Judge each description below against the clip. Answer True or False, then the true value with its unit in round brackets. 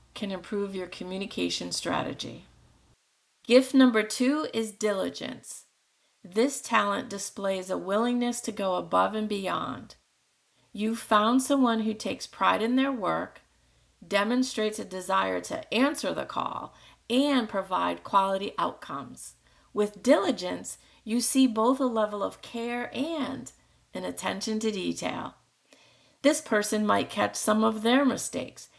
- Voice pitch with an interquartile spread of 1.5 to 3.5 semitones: False (3.9 semitones)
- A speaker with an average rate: False (130 wpm)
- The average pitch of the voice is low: False (220 Hz)